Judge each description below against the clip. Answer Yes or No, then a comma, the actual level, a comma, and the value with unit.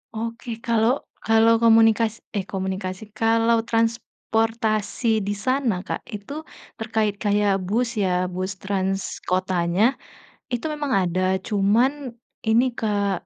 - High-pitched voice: Yes, high, 220 Hz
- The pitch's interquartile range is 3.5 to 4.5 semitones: No, average, 2.9 semitones